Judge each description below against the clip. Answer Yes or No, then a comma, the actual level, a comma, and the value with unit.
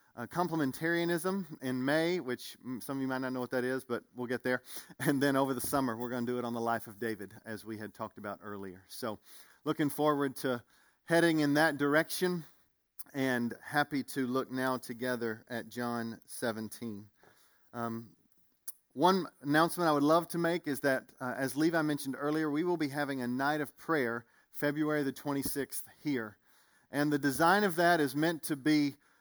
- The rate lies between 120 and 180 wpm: No, average, 190 wpm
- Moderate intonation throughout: Yes, average, 4.1 semitones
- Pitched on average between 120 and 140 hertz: Yes, low, 135 Hz